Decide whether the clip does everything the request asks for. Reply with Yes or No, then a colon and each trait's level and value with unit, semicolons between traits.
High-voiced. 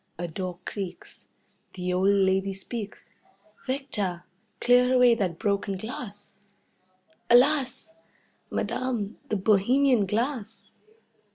Yes: high, 205 Hz